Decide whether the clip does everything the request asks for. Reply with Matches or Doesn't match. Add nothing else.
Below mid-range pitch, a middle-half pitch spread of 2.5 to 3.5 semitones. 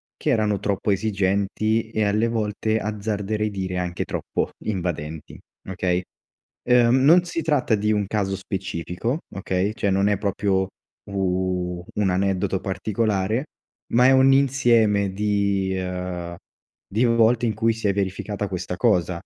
Matches